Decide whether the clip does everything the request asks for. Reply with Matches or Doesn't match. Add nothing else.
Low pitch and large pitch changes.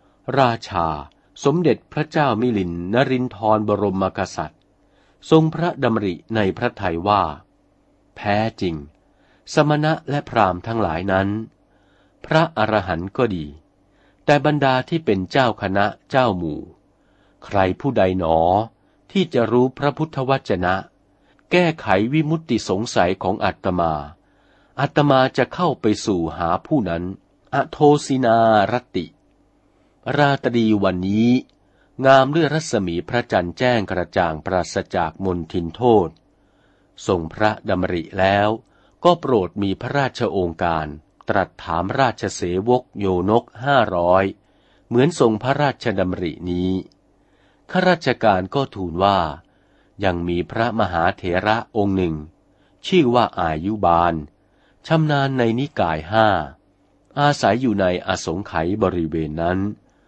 Matches